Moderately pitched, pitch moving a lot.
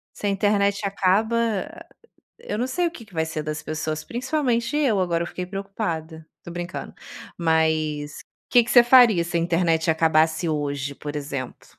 Yes: medium, 175 Hz; wide, 5.9 semitones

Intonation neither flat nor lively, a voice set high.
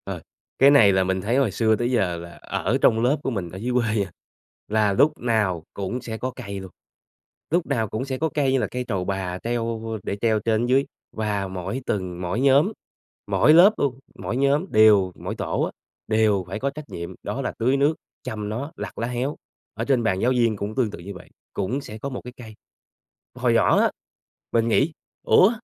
No: average, 4.7 semitones; low, 115 Hz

